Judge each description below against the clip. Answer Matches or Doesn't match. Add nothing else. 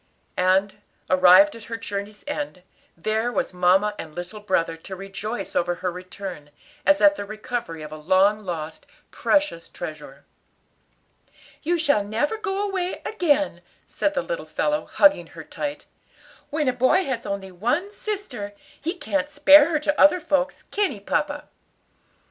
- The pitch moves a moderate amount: Doesn't match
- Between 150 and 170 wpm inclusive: Matches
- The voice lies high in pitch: Matches